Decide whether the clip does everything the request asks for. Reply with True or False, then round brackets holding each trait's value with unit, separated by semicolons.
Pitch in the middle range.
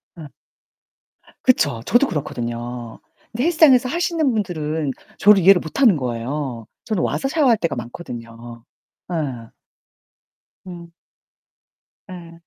True (165 Hz)